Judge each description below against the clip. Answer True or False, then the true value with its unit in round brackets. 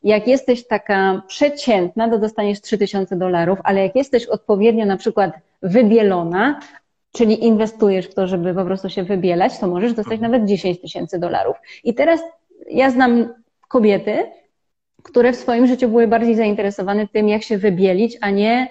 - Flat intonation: False (3.6 semitones)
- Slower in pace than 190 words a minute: True (160 wpm)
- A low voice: False (215 Hz)